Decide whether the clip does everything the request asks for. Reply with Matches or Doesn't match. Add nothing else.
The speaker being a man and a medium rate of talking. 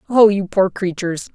Doesn't match